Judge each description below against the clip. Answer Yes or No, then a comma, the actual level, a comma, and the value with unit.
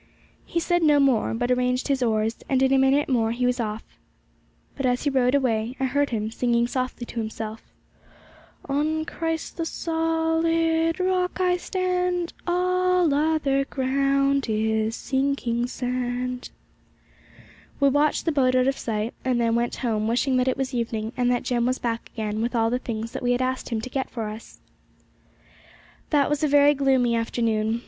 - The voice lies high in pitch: Yes, very high, 255 Hz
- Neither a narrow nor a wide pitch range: Yes, average, 3.7 semitones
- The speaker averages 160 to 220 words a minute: Yes, average, 175 wpm